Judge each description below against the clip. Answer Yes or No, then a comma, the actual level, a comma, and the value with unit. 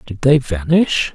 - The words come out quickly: No, average, 160 wpm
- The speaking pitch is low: Yes, low, 130 Hz